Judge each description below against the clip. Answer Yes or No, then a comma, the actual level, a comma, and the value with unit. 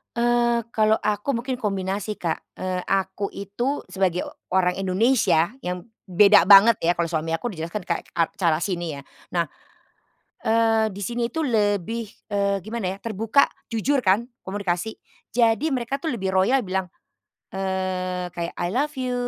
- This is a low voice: No, high, 200 Hz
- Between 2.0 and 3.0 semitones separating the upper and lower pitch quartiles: No, average, 4.2 semitones